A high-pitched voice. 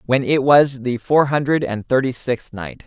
No: low, 130 Hz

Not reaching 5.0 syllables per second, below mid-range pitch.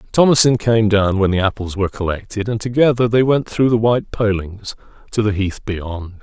No: 5.4 syllables/s; low, 105 Hz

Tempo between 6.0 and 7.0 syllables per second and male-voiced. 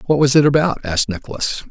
Yes: 6.5 syllables/s; male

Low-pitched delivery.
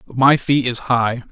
Yes: low, 125 Hz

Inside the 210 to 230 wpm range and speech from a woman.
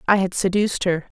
No: average, 200 wpm; female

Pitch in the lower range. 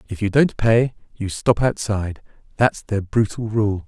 Yes: low, 105 Hz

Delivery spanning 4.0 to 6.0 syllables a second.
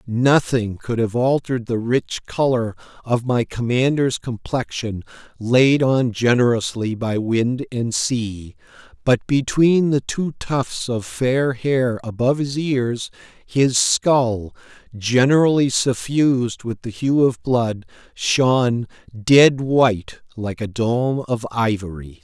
No: 3.6 syllables/s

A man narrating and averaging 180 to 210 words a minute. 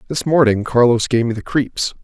Yes: male; fast, 205 wpm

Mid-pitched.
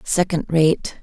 Yes: medium, 165 Hz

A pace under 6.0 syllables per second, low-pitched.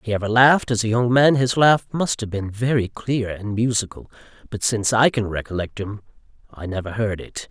Yes: 5.5 syllables/s; low, 115 Hz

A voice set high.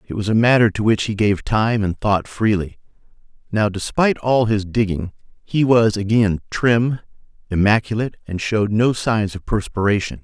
No: low, 105 Hz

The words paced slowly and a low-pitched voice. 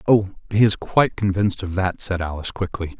No: average, 200 wpm; very low, 95 Hz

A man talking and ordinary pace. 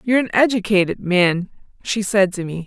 No: female; average, 180 wpm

